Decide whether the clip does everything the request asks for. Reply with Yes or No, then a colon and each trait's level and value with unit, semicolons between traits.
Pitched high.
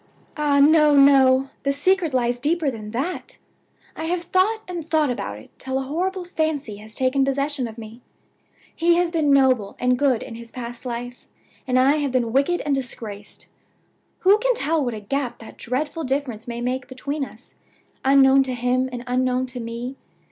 Yes: very high, 265 Hz